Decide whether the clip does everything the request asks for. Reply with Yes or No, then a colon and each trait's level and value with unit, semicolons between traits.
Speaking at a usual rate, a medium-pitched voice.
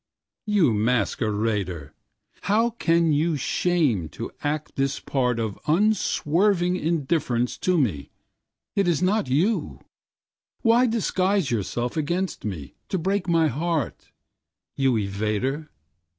No: slow, 95 wpm; medium, 150 Hz